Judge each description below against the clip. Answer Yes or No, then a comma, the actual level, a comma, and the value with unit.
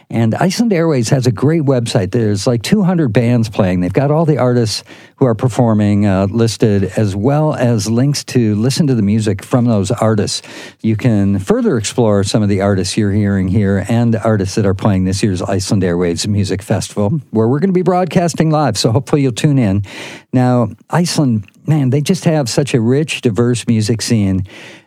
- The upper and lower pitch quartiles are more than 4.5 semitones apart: Yes, average, 5.0 semitones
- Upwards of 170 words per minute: Yes, average, 195 wpm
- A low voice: Yes, low, 120 Hz